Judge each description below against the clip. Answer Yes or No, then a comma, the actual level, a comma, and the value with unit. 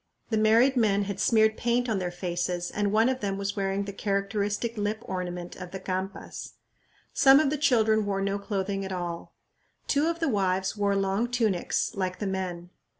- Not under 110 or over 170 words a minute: No, average, 190 wpm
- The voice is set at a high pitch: Yes, high, 200 Hz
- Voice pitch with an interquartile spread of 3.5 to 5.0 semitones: No, narrow, 2.6 semitones